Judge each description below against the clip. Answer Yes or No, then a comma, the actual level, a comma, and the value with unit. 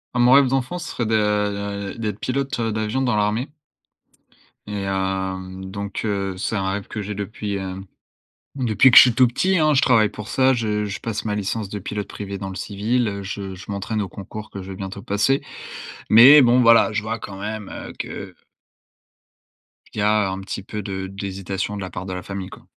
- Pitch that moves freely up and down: No, average, 2.7 semitones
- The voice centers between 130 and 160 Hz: No, low, 105 Hz